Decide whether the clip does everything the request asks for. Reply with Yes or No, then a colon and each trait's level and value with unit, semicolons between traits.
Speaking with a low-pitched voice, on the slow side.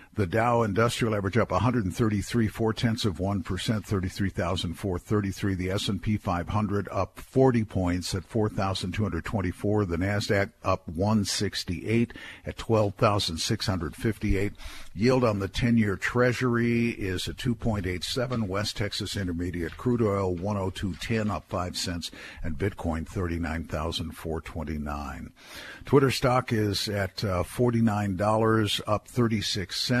Yes: low, 100 Hz; slow, 110 wpm